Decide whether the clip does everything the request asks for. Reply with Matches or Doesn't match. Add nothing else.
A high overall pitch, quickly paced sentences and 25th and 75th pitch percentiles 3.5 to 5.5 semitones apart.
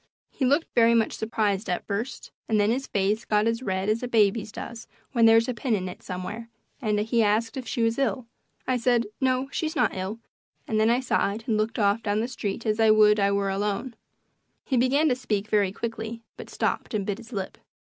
Doesn't match